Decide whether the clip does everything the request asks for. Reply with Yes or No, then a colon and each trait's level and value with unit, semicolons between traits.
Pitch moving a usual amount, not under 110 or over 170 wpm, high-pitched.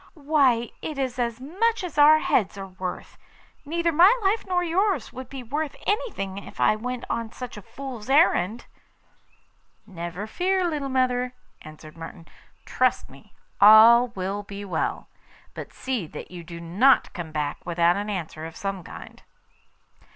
No: wide, 7.6 semitones; average, 160 wpm; high, 235 Hz